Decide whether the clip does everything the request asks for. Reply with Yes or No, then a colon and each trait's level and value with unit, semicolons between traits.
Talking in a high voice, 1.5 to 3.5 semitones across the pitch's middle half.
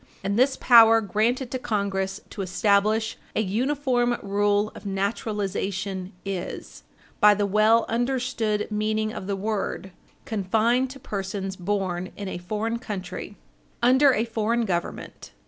Yes: high, 210 Hz; average, 3.0 semitones